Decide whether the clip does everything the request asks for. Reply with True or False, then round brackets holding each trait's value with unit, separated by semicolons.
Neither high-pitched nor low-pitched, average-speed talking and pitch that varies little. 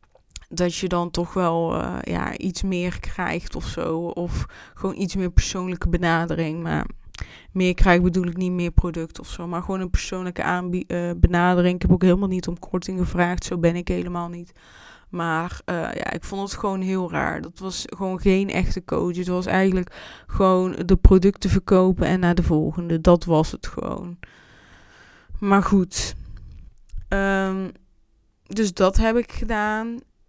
True (180 Hz; 170 wpm; 1.7 semitones)